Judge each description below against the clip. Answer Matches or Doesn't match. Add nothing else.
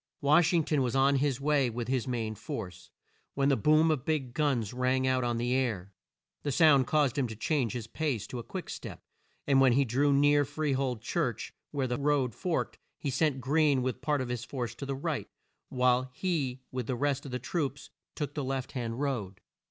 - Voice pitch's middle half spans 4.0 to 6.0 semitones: Doesn't match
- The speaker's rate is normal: Doesn't match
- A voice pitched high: Doesn't match